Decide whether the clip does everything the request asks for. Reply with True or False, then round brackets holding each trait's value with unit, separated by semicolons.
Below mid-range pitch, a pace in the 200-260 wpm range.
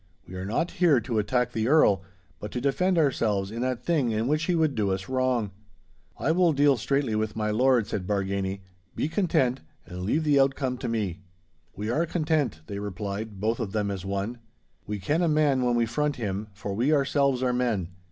True (120 Hz; 205 wpm)